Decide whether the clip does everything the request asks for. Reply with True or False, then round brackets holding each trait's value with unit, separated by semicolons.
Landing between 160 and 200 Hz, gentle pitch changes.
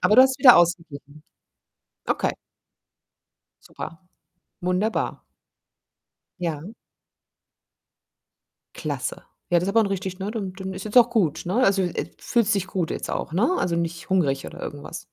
False (185 Hz; 3.8 semitones)